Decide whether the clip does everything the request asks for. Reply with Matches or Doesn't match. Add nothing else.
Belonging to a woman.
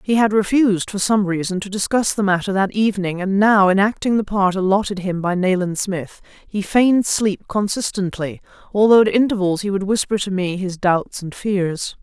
Matches